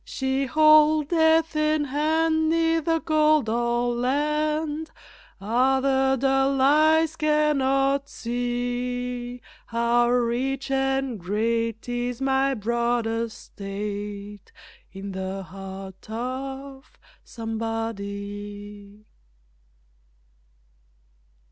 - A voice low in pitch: No, very high, 250 Hz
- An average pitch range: Yes, average, 4.5 semitones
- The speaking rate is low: Yes, slow, 75 wpm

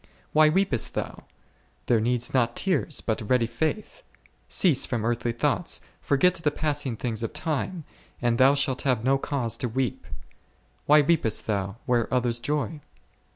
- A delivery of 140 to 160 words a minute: Yes, average, 155 wpm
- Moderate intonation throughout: Yes, average, 4.2 semitones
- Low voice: Yes, low, 130 Hz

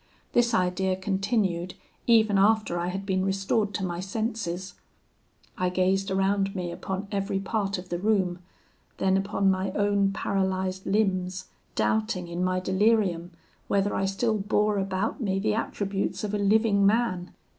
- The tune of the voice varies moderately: No, narrow, 1.9 semitones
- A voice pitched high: Yes, high, 195 Hz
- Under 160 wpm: Yes, average, 150 wpm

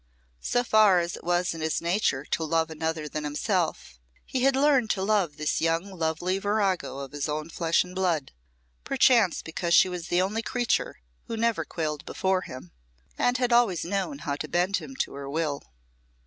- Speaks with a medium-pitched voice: Yes, medium, 175 Hz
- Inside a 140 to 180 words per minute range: No, average, 190 wpm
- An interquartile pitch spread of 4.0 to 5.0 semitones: Yes, average, 4.7 semitones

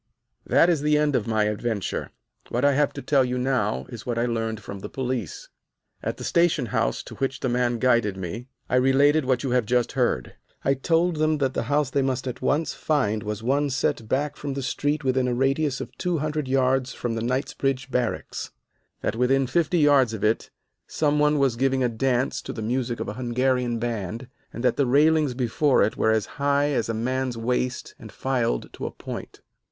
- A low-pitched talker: Yes, low, 130 Hz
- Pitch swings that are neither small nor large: Yes, average, 3.1 semitones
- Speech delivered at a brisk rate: Yes, fast, 210 wpm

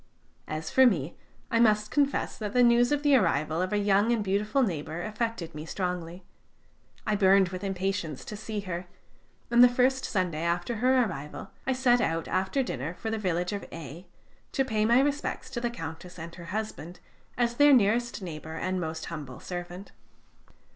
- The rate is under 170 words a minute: No, average, 180 wpm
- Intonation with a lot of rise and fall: Yes, wide, 5.8 semitones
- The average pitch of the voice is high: Yes, high, 195 Hz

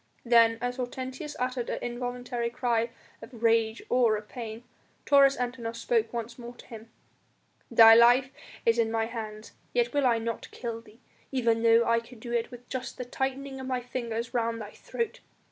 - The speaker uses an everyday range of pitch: No, narrow, 1.6 semitones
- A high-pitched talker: Yes, high, 235 Hz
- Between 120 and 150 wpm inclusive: No, average, 180 wpm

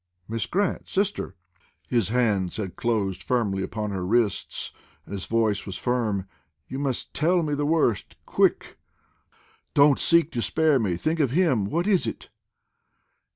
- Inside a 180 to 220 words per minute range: No, average, 155 wpm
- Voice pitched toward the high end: No, low, 120 Hz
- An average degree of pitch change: No, wide, 7.2 semitones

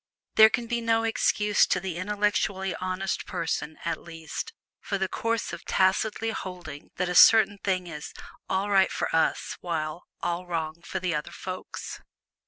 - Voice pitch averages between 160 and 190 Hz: Yes, medium, 185 Hz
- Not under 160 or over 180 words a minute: Yes, average, 165 wpm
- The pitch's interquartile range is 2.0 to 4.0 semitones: Yes, average, 3.3 semitones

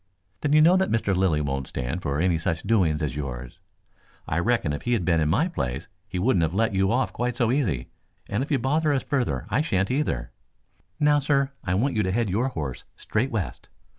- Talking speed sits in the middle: No, fast, 225 wpm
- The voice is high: No, low, 100 Hz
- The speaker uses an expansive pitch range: Yes, wide, 8.6 semitones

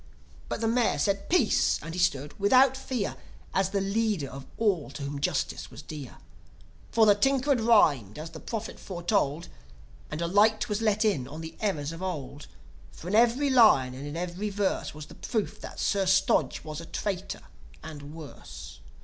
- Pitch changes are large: Yes, wide, 6.1 semitones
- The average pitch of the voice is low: No, high, 190 Hz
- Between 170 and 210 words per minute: Yes, average, 185 wpm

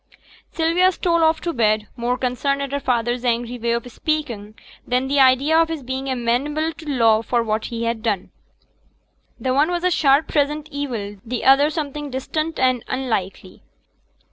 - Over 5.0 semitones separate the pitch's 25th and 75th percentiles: No, average, 4.2 semitones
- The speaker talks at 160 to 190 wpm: Yes, average, 175 wpm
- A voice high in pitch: Yes, very high, 260 Hz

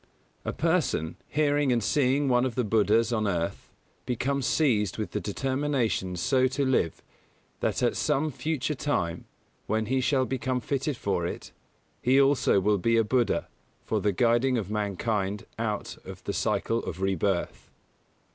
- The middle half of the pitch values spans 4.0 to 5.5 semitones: Yes, average, 4.4 semitones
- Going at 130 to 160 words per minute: Yes, average, 155 wpm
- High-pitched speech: No, low, 120 Hz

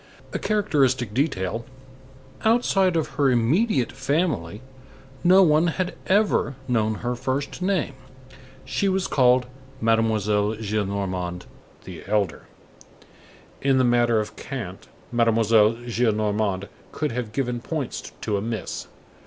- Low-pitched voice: Yes, low, 120 Hz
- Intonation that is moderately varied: No, wide, 5.7 semitones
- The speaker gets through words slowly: Yes, slow, 115 wpm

